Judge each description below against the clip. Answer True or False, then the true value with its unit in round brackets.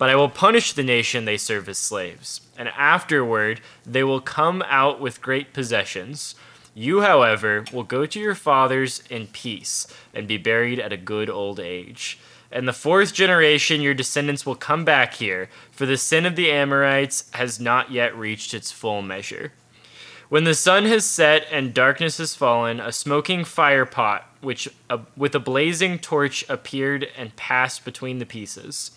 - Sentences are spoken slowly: False (175 wpm)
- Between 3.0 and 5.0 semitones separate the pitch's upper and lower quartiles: True (3.5 semitones)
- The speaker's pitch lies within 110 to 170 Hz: True (135 Hz)